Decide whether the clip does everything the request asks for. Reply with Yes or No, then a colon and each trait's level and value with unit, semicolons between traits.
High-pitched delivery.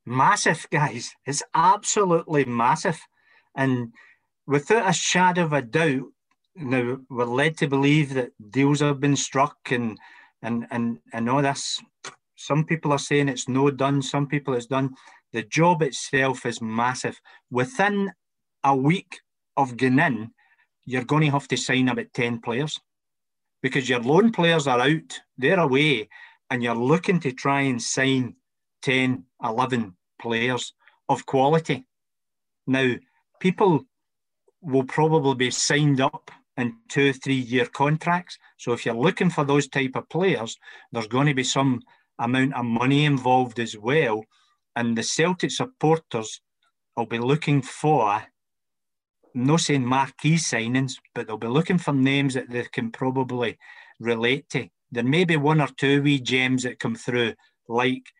No: low, 135 Hz